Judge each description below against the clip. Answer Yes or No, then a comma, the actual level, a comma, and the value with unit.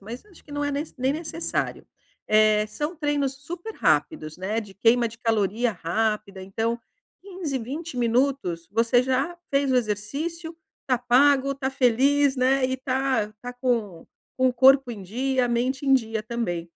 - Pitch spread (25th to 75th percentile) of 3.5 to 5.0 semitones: Yes, average, 3.8 semitones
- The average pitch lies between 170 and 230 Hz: No, very high, 255 Hz